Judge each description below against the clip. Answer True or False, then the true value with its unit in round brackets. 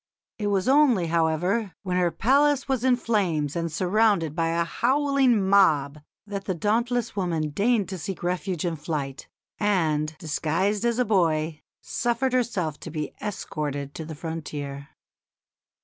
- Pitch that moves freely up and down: True (6.0 semitones)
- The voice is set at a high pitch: False (180 Hz)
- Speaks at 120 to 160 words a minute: True (150 wpm)